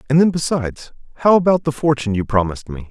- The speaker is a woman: No, male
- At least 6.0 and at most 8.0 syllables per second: Yes, 7.0 syllables/s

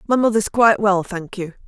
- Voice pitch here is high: Yes, high, 205 Hz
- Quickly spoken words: Yes, fast, 215 wpm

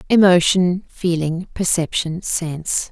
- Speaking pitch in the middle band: Yes, medium, 175 Hz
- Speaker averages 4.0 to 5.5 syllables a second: No, 3.8 syllables/s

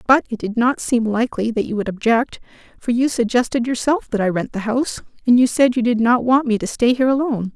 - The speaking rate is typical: No, fast, 245 wpm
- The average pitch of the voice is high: Yes, high, 235 Hz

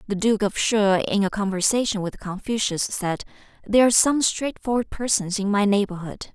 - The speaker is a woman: Yes, female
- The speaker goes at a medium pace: Yes, average, 170 wpm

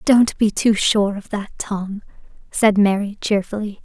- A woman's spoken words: Yes, female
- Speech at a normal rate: Yes, average, 155 wpm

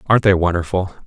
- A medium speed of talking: Yes, average, 170 wpm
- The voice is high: No, very low, 95 Hz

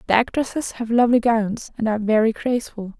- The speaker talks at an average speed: Yes, average, 180 wpm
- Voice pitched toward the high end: Yes, high, 225 Hz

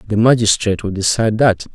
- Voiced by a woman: No, male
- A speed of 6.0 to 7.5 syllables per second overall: Yes, 6.6 syllables/s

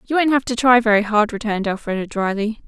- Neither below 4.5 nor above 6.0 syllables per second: No, 6.4 syllables/s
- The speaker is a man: No, female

